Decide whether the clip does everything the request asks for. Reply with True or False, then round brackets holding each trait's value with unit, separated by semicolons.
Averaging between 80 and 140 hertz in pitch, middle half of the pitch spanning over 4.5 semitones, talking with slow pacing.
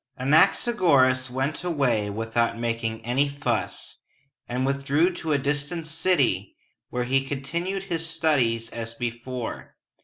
True (135 Hz; 5.1 semitones; 120 wpm)